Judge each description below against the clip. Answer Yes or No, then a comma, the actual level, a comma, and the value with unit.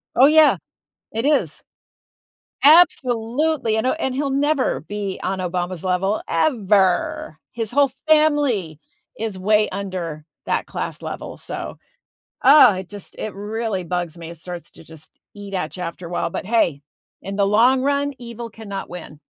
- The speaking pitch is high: Yes, high, 210 Hz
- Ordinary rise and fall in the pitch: No, wide, 6.1 semitones